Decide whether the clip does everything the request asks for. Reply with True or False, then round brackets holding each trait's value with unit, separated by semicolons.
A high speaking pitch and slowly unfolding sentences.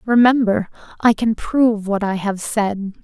False (215 Hz; 160 wpm)